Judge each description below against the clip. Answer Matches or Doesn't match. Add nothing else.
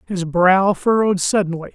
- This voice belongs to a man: Matches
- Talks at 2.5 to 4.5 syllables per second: Doesn't match